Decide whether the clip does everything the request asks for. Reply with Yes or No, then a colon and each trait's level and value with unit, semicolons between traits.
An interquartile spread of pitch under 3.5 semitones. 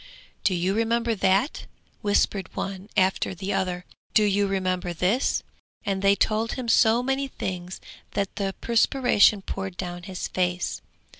Yes: average, 3.1 semitones